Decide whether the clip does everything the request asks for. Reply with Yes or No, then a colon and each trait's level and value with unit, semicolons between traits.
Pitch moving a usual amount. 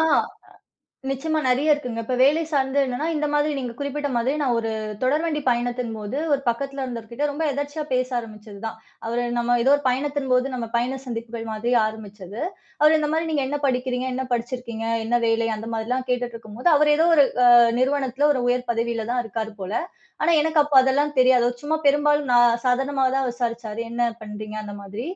Yes: average, 3.6 semitones